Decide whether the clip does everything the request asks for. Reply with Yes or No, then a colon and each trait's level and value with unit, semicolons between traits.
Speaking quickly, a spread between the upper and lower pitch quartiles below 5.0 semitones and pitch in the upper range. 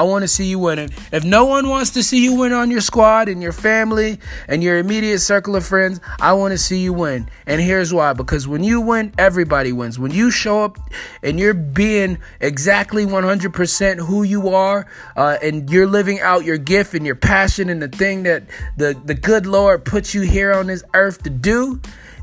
Yes: fast, 215 wpm; average, 3.8 semitones; high, 195 Hz